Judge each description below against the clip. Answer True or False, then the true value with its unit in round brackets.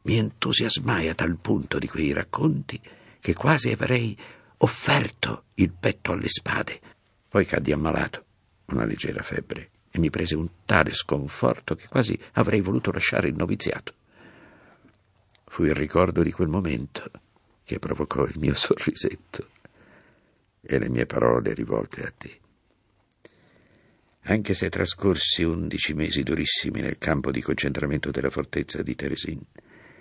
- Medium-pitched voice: False (80 Hz)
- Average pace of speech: True (135 wpm)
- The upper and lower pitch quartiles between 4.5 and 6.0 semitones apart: True (5.2 semitones)